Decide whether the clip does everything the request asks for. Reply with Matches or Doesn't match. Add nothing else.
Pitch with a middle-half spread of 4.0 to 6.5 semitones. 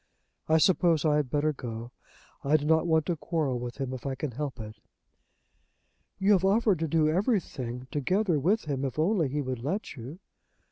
Matches